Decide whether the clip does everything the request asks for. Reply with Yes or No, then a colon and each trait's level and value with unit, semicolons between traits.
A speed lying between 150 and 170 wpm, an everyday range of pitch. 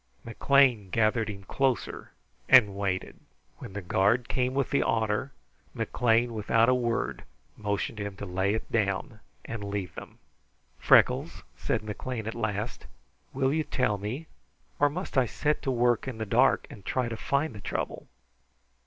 Yes: average, 160 wpm; average, 3.8 semitones